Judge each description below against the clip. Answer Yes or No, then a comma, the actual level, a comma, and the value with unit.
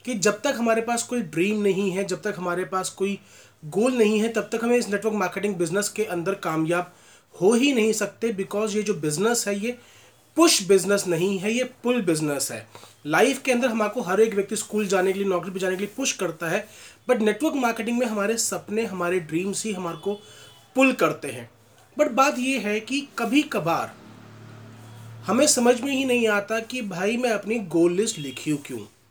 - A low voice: No, high, 205 Hz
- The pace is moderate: No, fast, 205 wpm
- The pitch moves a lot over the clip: No, average, 4.8 semitones